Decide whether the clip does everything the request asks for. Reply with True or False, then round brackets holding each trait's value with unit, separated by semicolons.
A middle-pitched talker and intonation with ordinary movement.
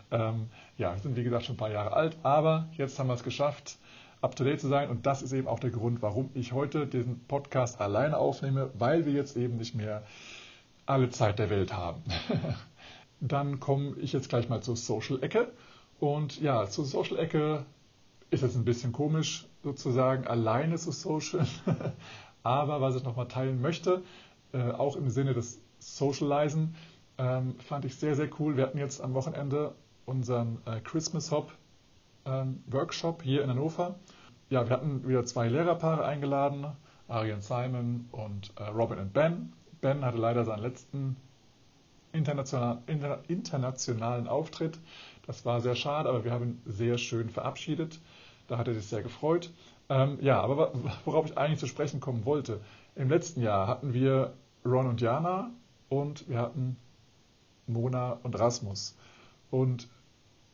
False (130 Hz; 3.3 semitones)